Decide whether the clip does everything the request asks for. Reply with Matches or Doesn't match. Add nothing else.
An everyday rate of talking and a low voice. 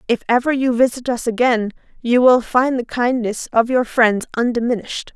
Doesn't match